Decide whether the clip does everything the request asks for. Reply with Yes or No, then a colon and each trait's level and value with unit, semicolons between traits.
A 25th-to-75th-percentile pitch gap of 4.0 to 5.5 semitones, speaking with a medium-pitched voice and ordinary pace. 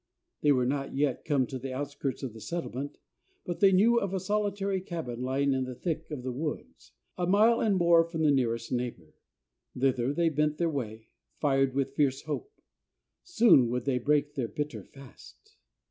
Yes: average, 4.9 semitones; medium, 145 Hz; average, 185 wpm